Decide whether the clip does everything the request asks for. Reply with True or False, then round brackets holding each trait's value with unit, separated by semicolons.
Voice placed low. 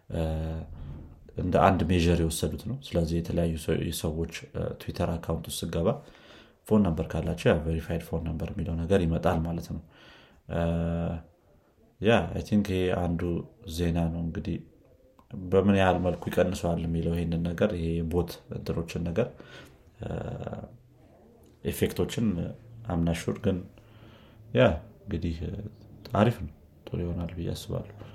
True (85 Hz)